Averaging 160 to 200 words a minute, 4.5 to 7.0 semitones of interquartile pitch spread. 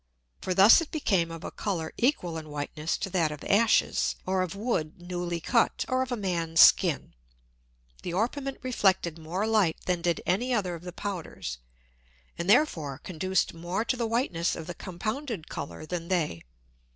Yes: average, 175 wpm; average, 4.8 semitones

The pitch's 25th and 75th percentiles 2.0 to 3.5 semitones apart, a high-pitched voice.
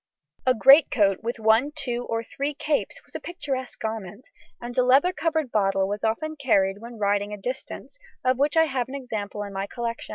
No: average, 4.8 semitones; high, 240 Hz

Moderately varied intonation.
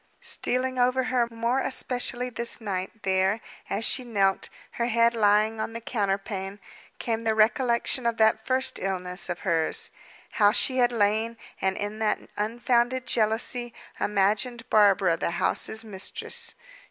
Yes: average, 3.0 semitones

